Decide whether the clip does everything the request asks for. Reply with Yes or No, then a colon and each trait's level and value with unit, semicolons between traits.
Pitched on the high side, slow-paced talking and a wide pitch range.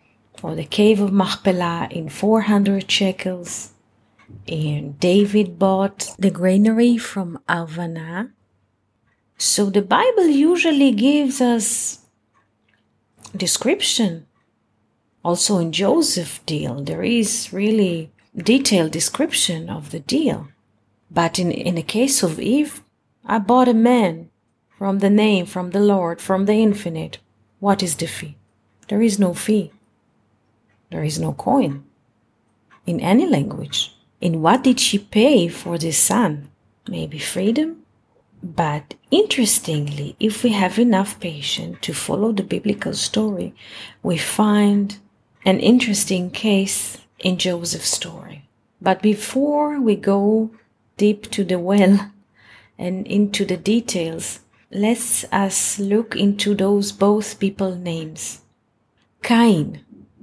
No: high, 195 Hz; slow, 120 wpm; average, 4.8 semitones